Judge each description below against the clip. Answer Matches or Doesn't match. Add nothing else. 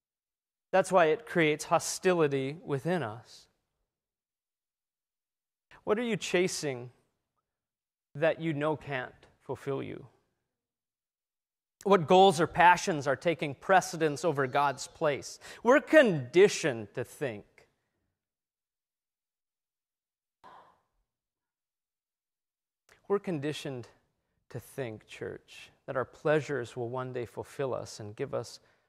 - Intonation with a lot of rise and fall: Matches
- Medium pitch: Matches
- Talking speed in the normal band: Doesn't match